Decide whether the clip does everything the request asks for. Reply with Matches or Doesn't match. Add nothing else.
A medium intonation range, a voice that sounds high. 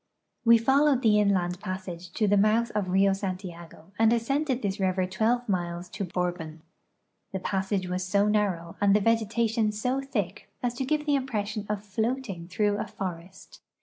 Matches